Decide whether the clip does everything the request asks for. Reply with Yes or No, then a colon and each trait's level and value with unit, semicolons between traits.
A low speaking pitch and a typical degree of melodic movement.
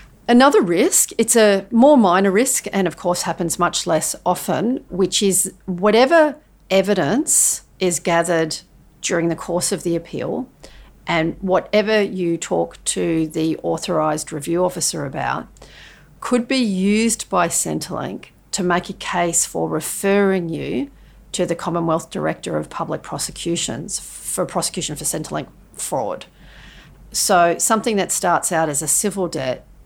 No: medium, 180 Hz; average, 3.4 semitones